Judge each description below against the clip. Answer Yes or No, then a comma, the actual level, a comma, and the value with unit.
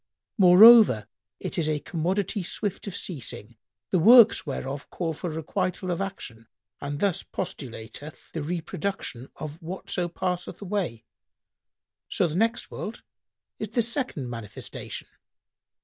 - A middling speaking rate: No, slow, 125 wpm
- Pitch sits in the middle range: Yes, medium, 175 Hz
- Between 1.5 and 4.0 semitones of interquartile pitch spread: No, average, 5.3 semitones